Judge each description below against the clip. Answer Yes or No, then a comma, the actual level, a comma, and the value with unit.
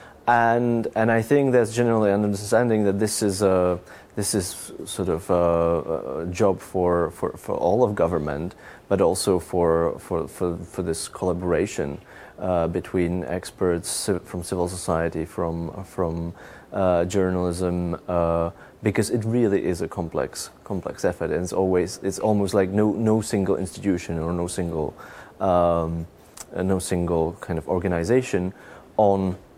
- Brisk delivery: No, average, 145 wpm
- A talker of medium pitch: No, very low, 90 Hz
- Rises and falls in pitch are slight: No, average, 3.3 semitones